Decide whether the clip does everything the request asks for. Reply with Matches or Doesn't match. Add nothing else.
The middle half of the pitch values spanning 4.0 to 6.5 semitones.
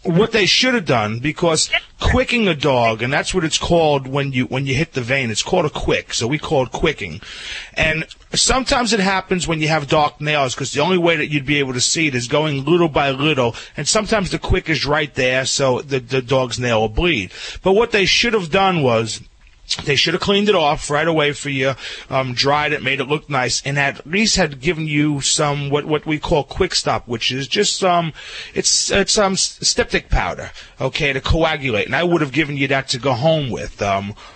Matches